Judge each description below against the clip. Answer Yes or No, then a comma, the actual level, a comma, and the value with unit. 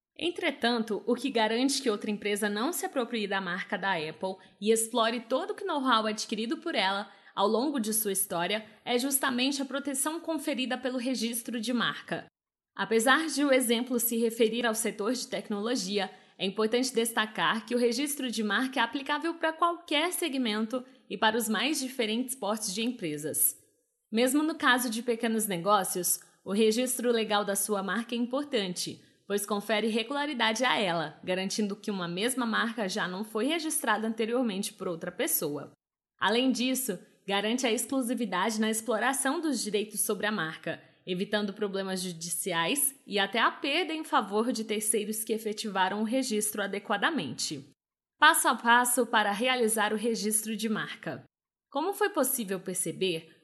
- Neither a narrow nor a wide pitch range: Yes, average, 3.9 semitones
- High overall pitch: Yes, high, 225 Hz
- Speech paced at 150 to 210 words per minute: Yes, average, 155 wpm